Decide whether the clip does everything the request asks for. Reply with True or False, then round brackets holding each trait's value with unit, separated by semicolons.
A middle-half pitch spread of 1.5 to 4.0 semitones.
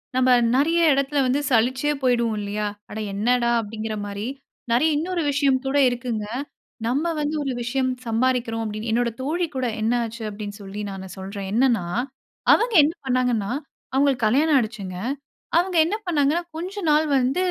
False (4.7 semitones)